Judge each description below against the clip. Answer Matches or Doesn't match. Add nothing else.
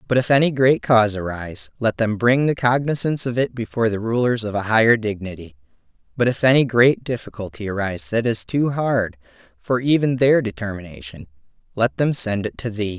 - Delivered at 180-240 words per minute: Matches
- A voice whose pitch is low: Matches